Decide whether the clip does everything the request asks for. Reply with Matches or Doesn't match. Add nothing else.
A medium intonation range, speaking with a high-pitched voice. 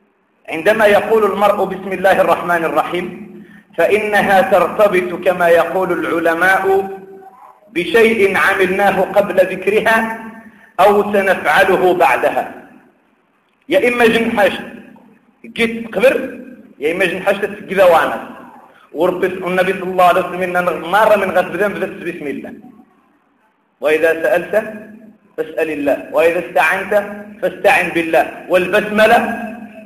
Matches